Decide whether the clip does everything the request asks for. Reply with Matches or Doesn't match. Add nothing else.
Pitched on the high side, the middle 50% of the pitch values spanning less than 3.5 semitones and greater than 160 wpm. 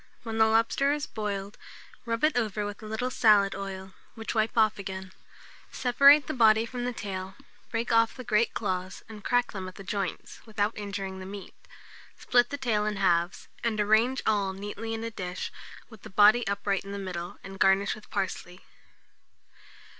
Matches